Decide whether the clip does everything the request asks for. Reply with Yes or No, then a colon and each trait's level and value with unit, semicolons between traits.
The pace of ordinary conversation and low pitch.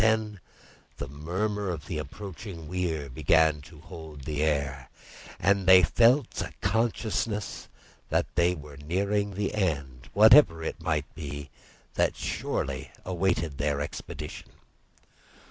No: slow, 125 wpm; very low, 85 Hz